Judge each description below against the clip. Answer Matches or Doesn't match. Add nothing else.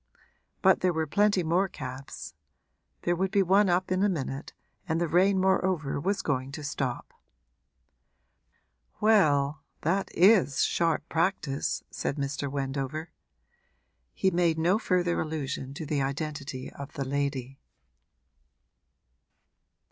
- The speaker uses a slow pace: Matches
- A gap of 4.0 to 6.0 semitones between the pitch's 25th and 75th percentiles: Matches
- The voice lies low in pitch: Doesn't match